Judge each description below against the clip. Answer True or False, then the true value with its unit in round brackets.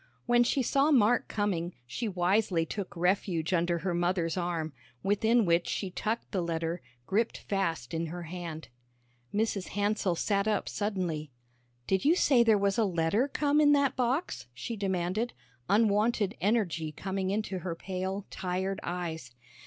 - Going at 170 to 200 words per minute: False (155 wpm)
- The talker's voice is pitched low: False (190 Hz)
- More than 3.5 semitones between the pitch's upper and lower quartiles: True (4.1 semitones)